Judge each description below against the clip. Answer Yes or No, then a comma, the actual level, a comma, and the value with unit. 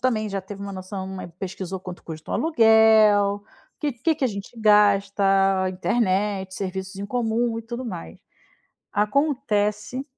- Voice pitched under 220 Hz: Yes, high, 205 Hz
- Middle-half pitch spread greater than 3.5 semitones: No, average, 2.9 semitones